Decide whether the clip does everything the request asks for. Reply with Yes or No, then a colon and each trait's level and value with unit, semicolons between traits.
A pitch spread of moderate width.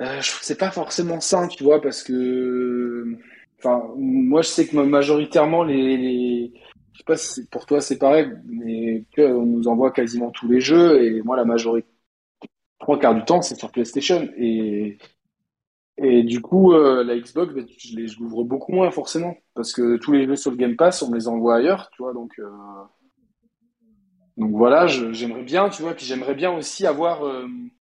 No: wide, 6.1 semitones